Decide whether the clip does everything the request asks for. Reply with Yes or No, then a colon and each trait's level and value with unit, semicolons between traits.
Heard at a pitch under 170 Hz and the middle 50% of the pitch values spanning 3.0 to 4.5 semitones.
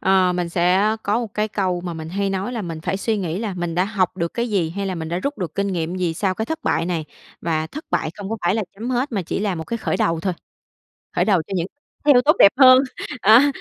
No: high, 190 Hz; average, 4.0 semitones